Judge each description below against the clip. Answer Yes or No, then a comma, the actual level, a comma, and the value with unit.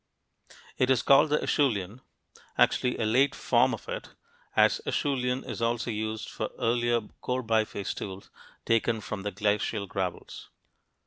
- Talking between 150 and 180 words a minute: No, average, 140 wpm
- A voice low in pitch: Yes, low, 115 Hz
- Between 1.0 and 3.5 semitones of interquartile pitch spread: Yes, average, 3.2 semitones